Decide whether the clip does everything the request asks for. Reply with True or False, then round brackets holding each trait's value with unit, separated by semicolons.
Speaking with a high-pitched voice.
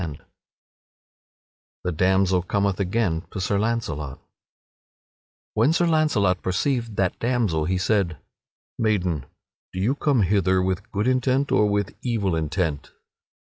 False (100 Hz)